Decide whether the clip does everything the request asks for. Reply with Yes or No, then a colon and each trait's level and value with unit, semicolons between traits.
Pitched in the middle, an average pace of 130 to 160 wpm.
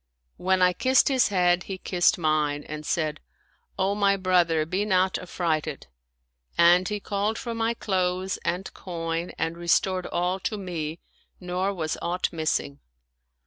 Yes: medium, 180 Hz; average, 155 wpm